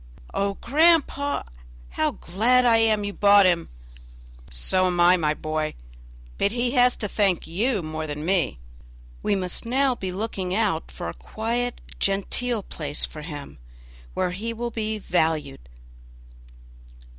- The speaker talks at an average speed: Yes, average, 145 wpm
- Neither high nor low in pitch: No, high, 195 Hz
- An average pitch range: No, wide, 6.0 semitones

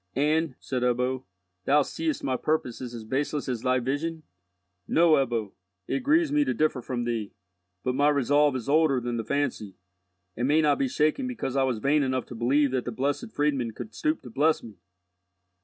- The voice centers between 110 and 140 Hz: Yes, low, 135 Hz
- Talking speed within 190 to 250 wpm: Yes, average, 195 wpm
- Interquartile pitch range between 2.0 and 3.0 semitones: No, average, 3.6 semitones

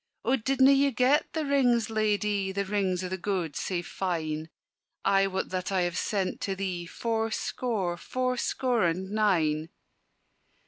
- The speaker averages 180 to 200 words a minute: No, average, 155 wpm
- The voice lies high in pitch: Yes, high, 195 Hz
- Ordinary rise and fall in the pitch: Yes, average, 4.3 semitones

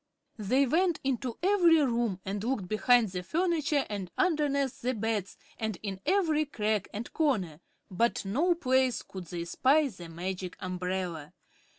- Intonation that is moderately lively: No, wide, 7.3 semitones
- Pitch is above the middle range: Yes, high, 235 Hz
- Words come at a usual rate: Yes, average, 150 wpm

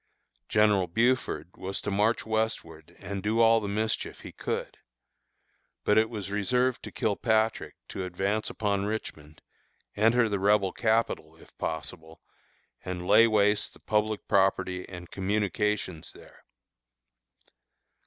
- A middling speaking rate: No, slow, 125 wpm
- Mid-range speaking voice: No, low, 105 Hz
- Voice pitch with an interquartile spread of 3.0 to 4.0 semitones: No, narrow, 2.6 semitones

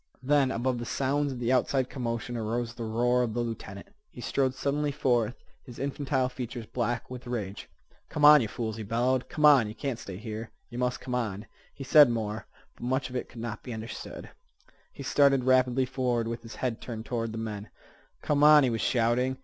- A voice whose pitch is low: Yes, low, 120 Hz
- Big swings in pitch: No, narrow, 2.4 semitones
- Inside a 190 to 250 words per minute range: Yes, fast, 205 wpm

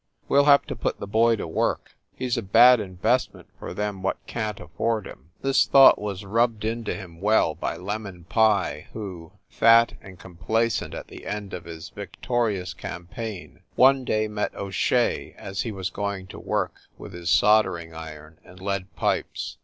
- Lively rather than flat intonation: No, average, 3.9 semitones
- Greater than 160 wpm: Yes, average, 185 wpm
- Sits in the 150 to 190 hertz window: No, low, 100 Hz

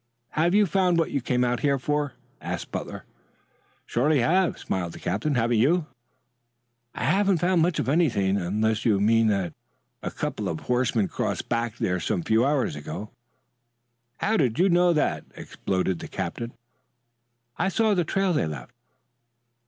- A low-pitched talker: Yes, low, 125 Hz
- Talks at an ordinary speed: Yes, average, 160 wpm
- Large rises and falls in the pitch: Yes, wide, 8.3 semitones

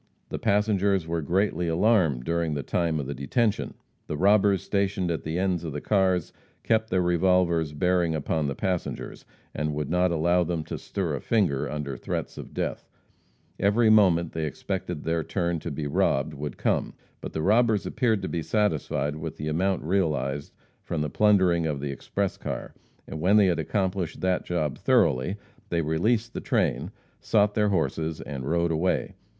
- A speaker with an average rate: Yes, average, 180 wpm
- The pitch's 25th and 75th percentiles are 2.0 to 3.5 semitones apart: No, average, 4.1 semitones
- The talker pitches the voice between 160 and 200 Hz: No, very low, 85 Hz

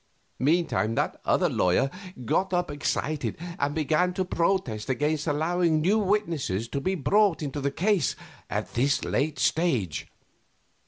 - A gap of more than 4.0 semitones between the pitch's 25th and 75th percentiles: Yes, average, 4.5 semitones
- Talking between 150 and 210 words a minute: No, average, 140 wpm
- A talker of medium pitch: Yes, medium, 155 Hz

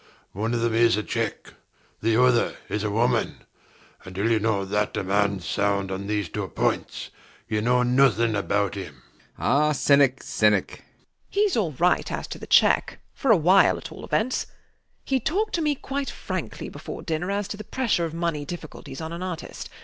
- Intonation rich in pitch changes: Yes, wide, 8.9 semitones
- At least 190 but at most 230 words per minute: Yes, average, 195 wpm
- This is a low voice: Yes, low, 125 Hz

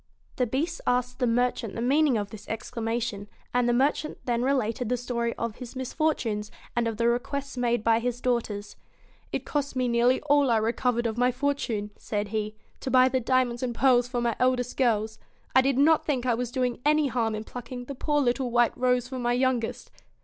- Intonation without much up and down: Yes, narrow, 1.9 semitones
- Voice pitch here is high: Yes, high, 245 Hz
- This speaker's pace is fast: Yes, fast, 210 wpm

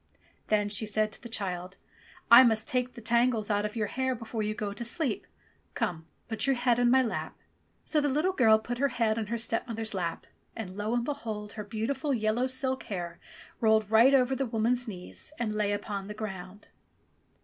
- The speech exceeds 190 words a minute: Yes, average, 200 wpm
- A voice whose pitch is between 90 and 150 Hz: No, high, 225 Hz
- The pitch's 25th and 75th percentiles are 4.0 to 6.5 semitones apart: No, average, 2.9 semitones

